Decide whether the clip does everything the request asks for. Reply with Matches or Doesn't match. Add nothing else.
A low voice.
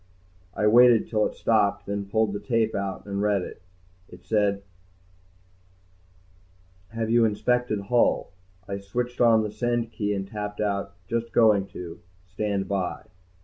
Matches